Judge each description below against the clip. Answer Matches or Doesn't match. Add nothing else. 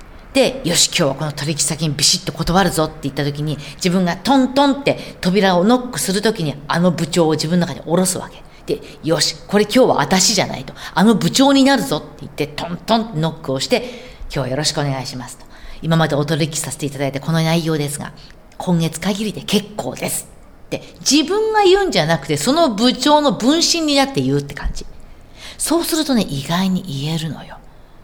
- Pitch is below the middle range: Doesn't match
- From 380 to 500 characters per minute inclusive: Matches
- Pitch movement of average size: Doesn't match